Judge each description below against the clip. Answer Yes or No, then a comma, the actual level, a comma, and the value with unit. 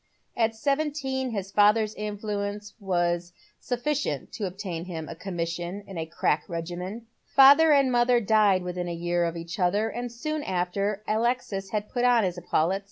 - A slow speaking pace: No, average, 165 wpm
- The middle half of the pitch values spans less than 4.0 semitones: No, average, 5.2 semitones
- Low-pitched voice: No, high, 205 Hz